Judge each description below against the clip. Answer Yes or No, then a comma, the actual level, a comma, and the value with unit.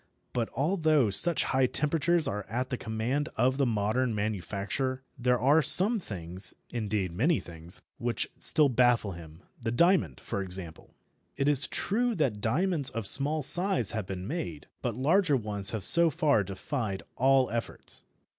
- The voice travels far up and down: Yes, wide, 6.3 semitones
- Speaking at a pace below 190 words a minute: Yes, average, 155 wpm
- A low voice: Yes, low, 125 Hz